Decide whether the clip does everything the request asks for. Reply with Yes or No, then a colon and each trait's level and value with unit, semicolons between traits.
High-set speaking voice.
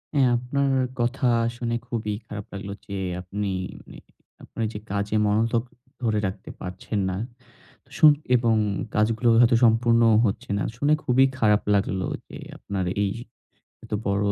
No: low, 110 Hz